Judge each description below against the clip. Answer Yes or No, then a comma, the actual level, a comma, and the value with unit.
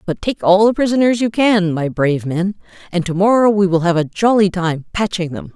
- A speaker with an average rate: No, fast, 225 wpm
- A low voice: No, high, 190 Hz